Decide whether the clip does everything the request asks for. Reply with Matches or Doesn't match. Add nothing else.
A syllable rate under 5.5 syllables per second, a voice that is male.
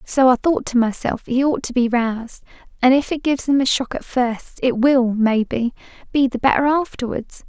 Doesn't match